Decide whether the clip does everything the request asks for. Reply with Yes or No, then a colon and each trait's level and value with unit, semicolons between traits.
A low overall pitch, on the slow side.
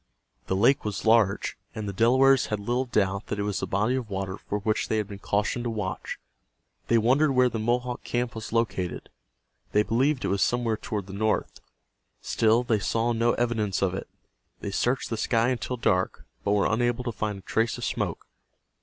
No: low, 110 Hz; average, 200 wpm